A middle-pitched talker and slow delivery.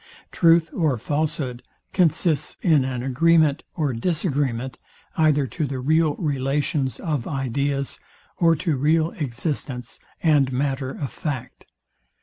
Yes: medium, 145 Hz; slow, 120 wpm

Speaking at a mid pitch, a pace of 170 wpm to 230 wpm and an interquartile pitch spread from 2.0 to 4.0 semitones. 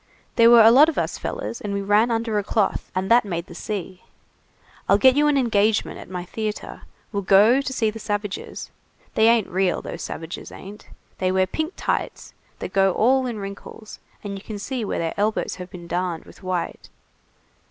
No: high, 205 Hz; average, 200 wpm; average, 3.6 semitones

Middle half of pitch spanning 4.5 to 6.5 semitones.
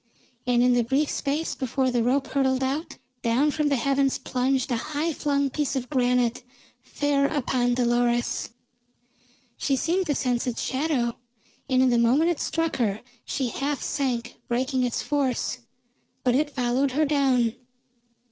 No: average, 2.7 semitones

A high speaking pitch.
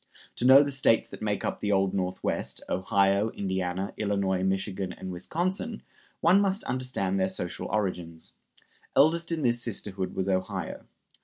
No: low, 100 Hz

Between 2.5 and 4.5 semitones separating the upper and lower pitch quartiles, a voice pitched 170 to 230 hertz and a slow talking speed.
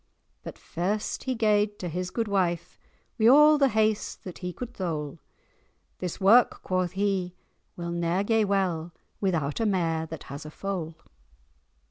No: average, 3.7 semitones; medium, 185 Hz; average, 155 wpm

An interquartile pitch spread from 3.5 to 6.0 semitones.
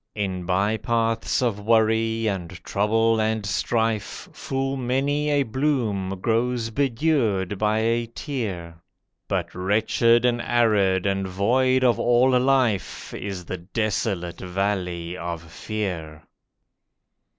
Yes: average, 3.9 semitones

